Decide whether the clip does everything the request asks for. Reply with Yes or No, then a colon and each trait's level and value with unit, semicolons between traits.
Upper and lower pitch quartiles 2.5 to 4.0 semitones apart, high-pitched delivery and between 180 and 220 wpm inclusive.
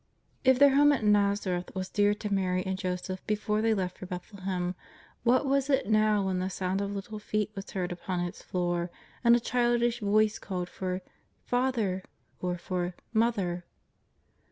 Yes: average, 3.4 semitones; high, 200 Hz; average, 190 wpm